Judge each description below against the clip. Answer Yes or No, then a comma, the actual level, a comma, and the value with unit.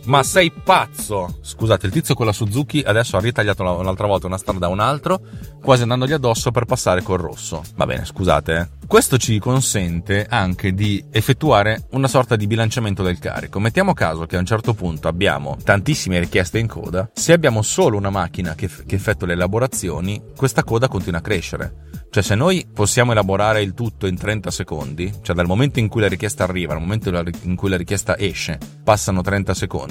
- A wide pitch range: No, average, 4.2 semitones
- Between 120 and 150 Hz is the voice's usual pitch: No, low, 100 Hz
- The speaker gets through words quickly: Yes, fast, 195 wpm